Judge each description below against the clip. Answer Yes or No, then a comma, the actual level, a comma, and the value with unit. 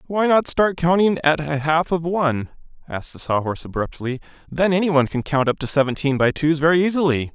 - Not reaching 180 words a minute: No, fast, 205 wpm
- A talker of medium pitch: Yes, medium, 155 Hz